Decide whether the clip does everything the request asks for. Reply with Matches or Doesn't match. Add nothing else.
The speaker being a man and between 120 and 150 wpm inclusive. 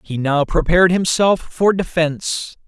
Matches